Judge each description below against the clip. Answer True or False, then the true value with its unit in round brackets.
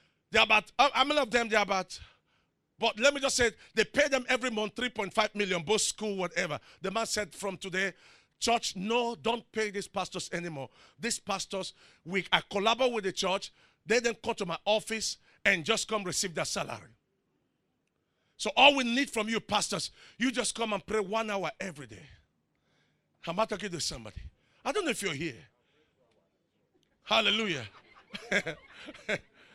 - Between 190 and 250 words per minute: False (175 wpm)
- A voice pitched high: True (210 Hz)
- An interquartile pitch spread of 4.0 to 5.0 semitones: False (3.5 semitones)